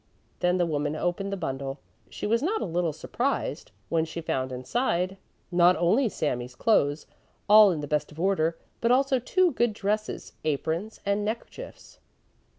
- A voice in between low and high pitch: Yes, medium, 180 Hz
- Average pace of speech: Yes, average, 160 wpm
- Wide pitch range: Yes, wide, 5.8 semitones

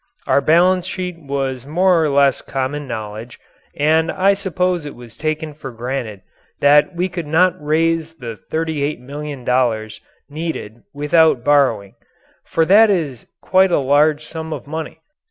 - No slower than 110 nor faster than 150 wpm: Yes, average, 140 wpm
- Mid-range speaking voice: Yes, medium, 150 Hz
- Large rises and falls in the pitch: No, average, 3.8 semitones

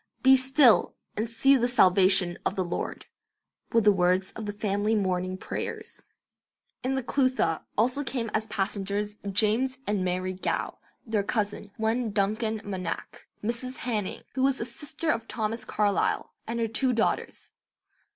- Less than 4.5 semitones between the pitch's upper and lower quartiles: Yes, average, 3.7 semitones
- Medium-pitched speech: No, high, 215 Hz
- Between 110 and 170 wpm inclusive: Yes, average, 150 wpm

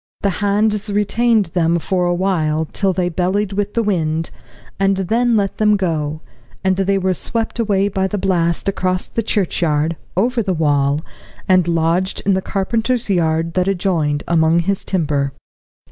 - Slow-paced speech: No, average, 160 wpm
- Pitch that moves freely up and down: No, average, 3.5 semitones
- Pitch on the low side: No, medium, 185 Hz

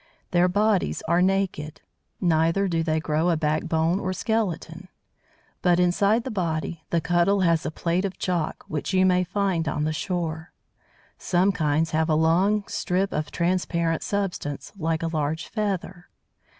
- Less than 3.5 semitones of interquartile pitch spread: Yes, average, 2.8 semitones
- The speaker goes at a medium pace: Yes, average, 155 wpm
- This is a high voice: No, medium, 175 Hz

